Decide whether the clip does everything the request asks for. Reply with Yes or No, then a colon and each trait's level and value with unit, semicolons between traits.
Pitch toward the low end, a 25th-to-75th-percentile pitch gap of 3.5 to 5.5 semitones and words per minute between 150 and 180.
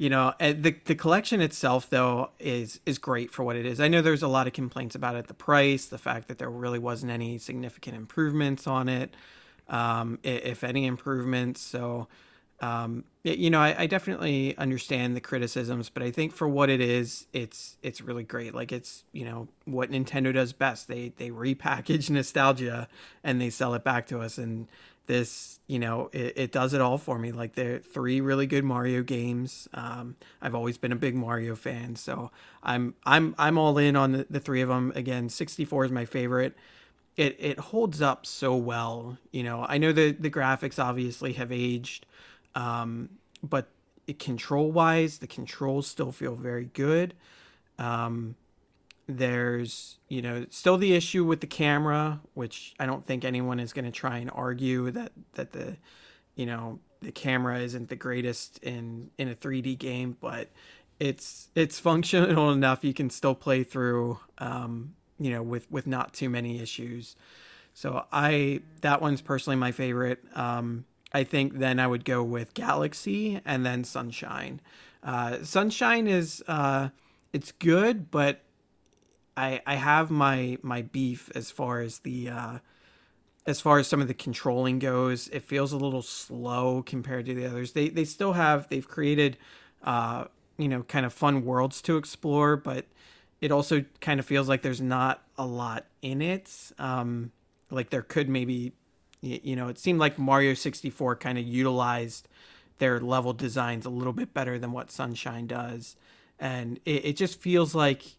No: low, 130 Hz; average, 2.7 semitones; average, 175 wpm